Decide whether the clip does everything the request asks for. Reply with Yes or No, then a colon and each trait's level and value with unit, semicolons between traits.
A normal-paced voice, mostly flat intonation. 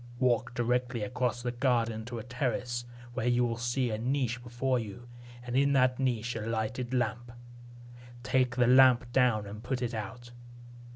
Yes: average, 170 wpm; narrow, 1.3 semitones